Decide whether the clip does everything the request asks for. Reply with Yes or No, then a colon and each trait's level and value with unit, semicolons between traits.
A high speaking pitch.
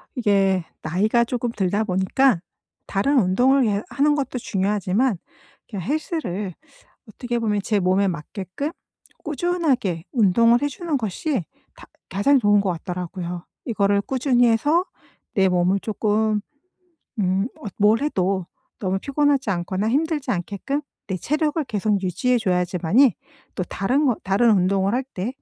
Yes: high, 210 Hz